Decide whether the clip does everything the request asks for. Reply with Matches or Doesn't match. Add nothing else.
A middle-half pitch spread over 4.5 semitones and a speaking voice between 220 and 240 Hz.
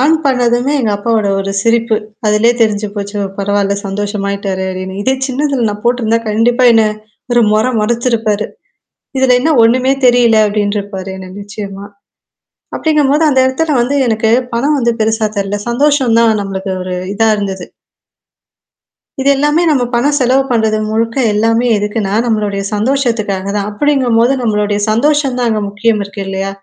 Doesn't match